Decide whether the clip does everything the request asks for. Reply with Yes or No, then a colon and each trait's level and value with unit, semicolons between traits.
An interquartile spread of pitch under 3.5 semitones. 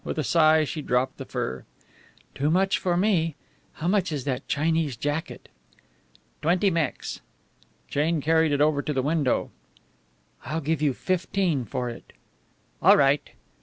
Yes: average, 2.8 semitones